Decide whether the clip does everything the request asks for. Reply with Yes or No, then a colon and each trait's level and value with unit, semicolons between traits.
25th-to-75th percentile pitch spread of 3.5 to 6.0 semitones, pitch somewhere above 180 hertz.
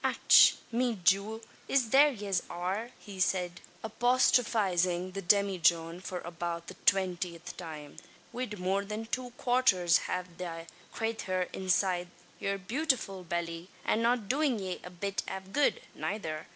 Yes: average, 4.1 semitones; high, 190 Hz